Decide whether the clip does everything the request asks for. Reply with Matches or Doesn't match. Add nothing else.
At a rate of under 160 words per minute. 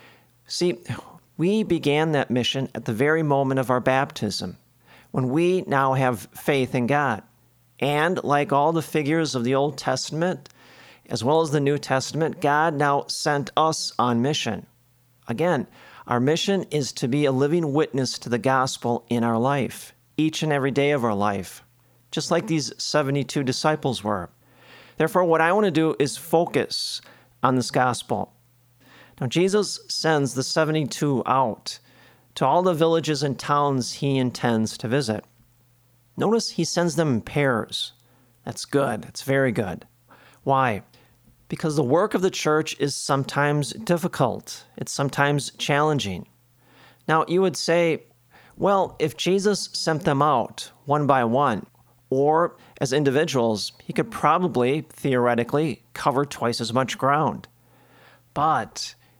Matches